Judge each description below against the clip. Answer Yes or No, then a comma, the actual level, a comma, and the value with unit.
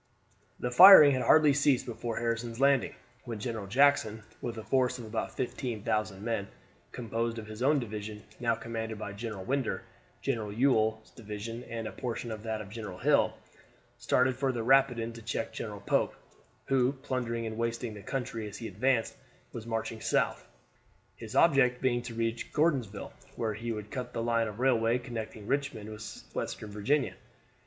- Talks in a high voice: No, low, 115 Hz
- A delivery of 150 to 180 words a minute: Yes, average, 170 wpm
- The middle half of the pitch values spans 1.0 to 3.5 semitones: Yes, average, 2.7 semitones